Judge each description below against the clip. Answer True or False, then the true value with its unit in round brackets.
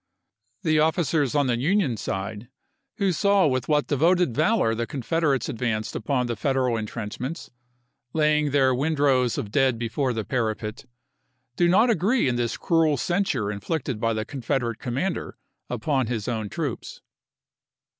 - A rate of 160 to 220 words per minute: False (145 wpm)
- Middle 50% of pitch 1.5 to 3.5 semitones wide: False (5.2 semitones)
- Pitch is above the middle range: False (130 Hz)